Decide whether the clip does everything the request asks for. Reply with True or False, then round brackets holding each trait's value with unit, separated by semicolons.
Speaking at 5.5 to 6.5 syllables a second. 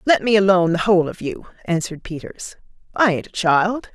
True (5.8 syllables/s)